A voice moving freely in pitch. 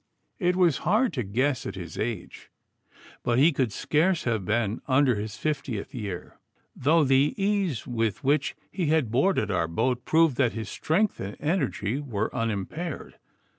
Yes: wide, 6.3 semitones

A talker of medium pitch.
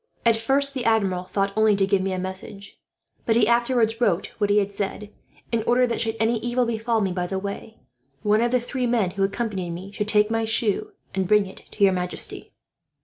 No: high, 210 Hz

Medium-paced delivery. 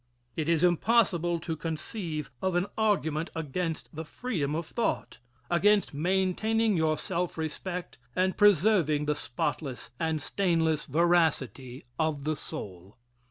No: slow, 125 wpm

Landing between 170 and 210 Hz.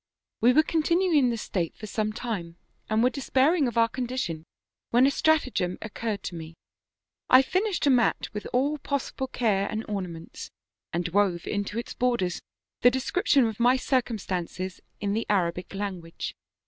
No: high, 225 Hz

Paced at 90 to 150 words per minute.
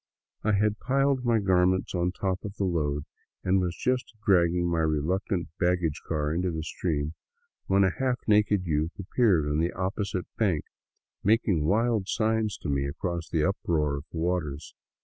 No: average, 170 wpm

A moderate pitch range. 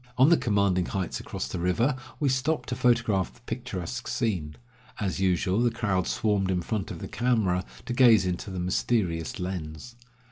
Yes: average, 4.9 semitones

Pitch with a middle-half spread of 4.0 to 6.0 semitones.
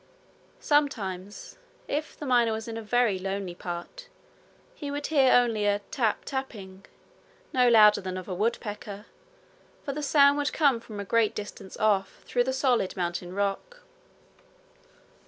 Yes: average, 5.3 semitones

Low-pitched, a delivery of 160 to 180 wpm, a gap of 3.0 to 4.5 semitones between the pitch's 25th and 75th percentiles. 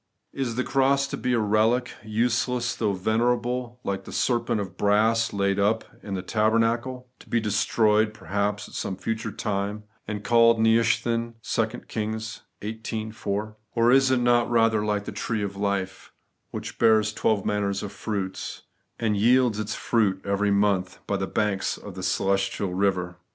No: low, 110 Hz; average, 165 wpm; narrow, 2.5 semitones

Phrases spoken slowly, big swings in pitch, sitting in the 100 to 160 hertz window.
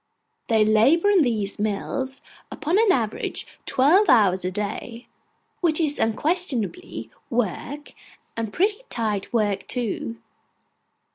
No: slow, 115 wpm; wide, 6.9 semitones; high, 240 Hz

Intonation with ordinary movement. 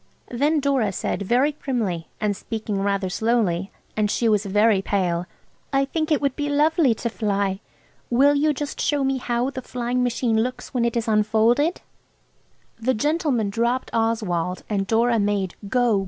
Yes: average, 4.5 semitones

